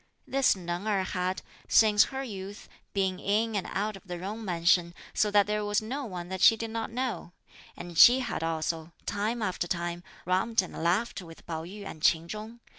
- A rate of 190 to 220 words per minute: Yes, average, 195 wpm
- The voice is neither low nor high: No, high, 195 Hz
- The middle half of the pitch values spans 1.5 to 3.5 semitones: No, average, 3.9 semitones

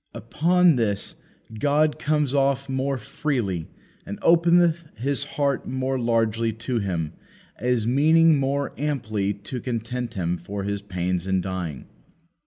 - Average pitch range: No, wide, 5.9 semitones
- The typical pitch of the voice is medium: No, low, 125 Hz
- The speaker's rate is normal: No, slow, 130 wpm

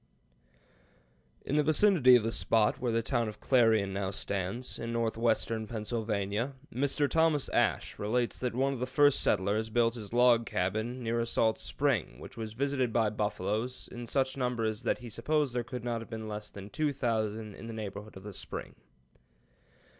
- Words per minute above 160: Yes, average, 185 wpm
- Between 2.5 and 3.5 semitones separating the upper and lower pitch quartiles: Yes, average, 2.8 semitones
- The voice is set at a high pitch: No, low, 115 Hz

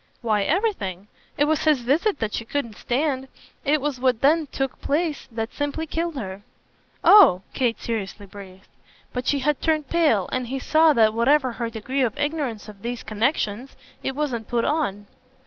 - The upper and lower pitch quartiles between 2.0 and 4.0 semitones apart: No, average, 5.1 semitones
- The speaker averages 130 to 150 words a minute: No, average, 175 wpm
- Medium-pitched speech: No, very high, 260 Hz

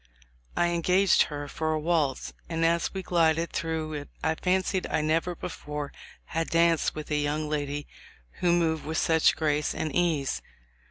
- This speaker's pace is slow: No, average, 165 wpm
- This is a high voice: No, medium, 160 Hz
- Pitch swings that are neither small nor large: No, narrow, 2.1 semitones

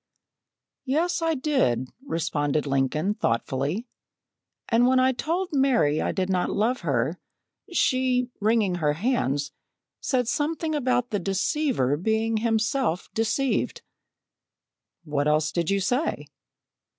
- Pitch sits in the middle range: No, high, 220 Hz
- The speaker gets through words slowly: Yes, slow, 115 wpm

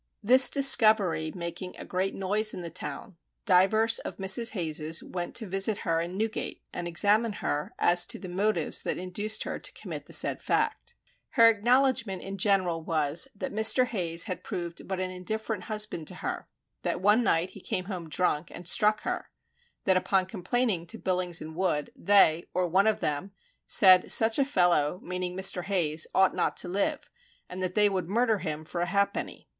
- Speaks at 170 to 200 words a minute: Yes, average, 190 wpm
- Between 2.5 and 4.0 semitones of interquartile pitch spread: Yes, average, 3.5 semitones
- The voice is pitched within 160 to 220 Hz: Yes, medium, 185 Hz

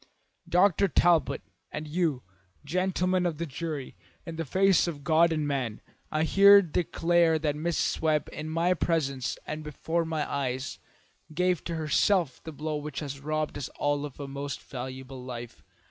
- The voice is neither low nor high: Yes, medium, 155 Hz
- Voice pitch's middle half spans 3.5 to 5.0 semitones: No, average, 3.1 semitones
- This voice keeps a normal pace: Yes, average, 160 wpm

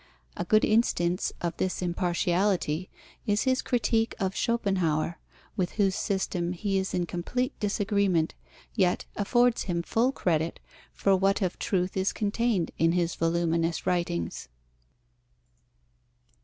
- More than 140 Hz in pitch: Yes, medium, 185 Hz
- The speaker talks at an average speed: No, slow, 125 wpm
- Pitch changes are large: No, average, 3.2 semitones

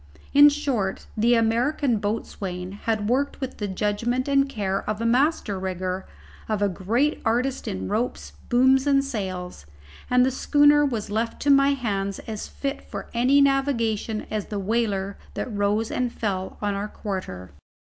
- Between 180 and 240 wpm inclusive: No, average, 160 wpm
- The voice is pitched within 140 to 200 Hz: No, high, 225 Hz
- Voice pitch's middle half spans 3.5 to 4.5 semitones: No, average, 4.9 semitones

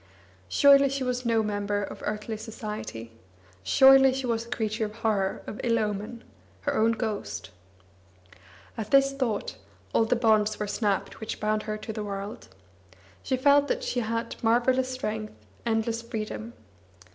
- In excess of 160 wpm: No, average, 155 wpm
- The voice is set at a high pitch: Yes, high, 225 Hz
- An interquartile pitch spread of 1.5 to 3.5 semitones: Yes, average, 2.8 semitones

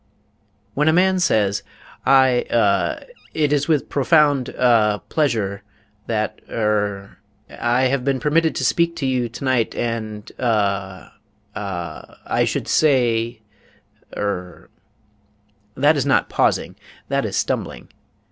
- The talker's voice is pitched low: Yes, low, 120 Hz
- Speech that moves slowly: Yes, slow, 120 wpm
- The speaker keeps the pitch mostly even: No, average, 5.2 semitones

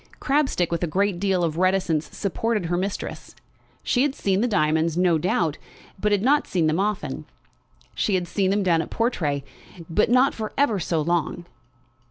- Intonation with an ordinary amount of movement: Yes, average, 4.0 semitones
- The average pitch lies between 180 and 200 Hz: Yes, medium, 185 Hz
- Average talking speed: Yes, average, 180 wpm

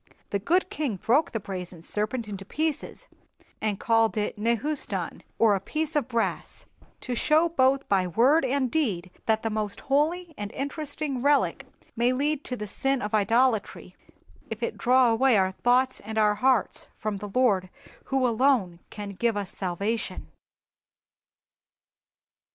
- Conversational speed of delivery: Yes, average, 150 wpm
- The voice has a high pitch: Yes, high, 235 Hz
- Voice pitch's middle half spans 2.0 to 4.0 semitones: No, average, 4.7 semitones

